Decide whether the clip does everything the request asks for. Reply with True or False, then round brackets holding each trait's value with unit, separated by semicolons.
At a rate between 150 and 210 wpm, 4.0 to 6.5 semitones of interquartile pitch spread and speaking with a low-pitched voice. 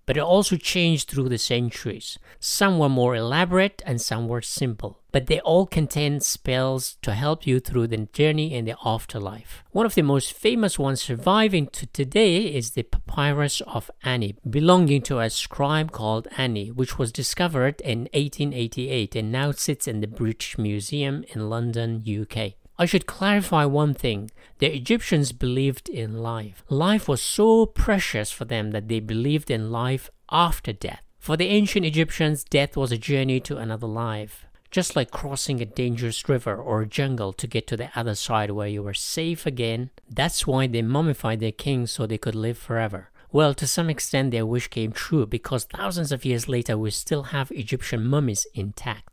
True (180 wpm; 4.6 semitones; 130 Hz)